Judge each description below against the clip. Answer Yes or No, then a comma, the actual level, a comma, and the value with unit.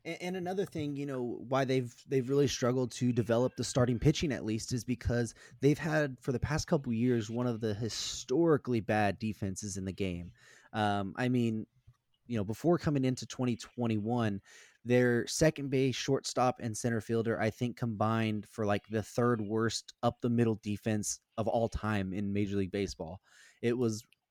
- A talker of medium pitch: No, low, 120 Hz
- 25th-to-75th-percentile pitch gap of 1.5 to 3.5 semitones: Yes, average, 3.0 semitones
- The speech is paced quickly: No, average, 180 wpm